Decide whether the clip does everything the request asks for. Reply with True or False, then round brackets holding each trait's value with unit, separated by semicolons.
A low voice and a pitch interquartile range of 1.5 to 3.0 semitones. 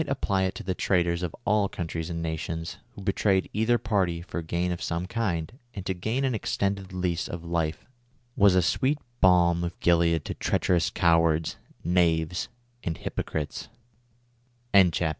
True (90 Hz; 2.7 semitones)